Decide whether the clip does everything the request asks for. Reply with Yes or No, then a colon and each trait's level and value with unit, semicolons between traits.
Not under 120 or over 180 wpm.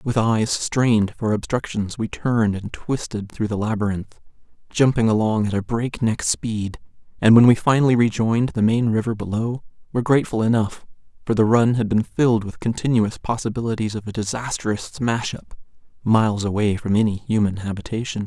Yes: average, 165 wpm